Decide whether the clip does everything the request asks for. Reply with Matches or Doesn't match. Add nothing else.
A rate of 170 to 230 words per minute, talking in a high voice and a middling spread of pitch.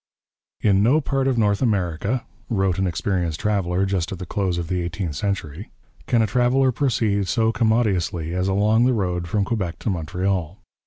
Doesn't match